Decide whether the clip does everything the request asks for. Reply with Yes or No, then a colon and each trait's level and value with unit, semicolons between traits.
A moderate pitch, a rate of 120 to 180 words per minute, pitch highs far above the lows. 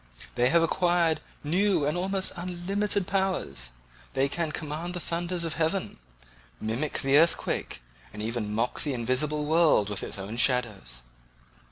Yes: medium, 155 Hz; average, 145 wpm; wide, 6.3 semitones